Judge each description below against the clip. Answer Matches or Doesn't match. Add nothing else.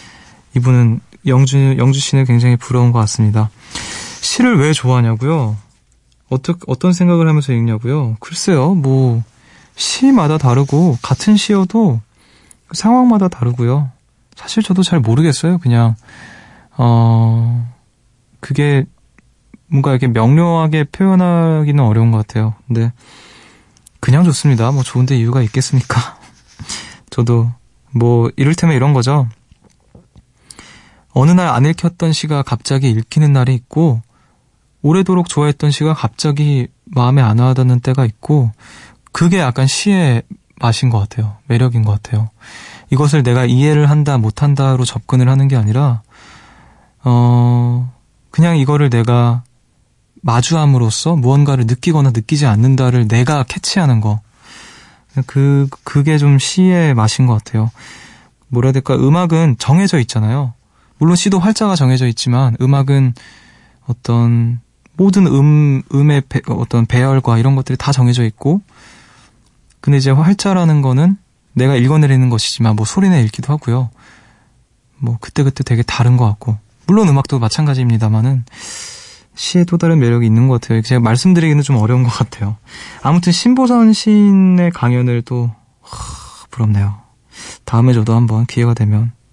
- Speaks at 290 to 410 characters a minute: Matches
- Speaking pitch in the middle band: Doesn't match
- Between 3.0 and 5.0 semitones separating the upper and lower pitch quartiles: Matches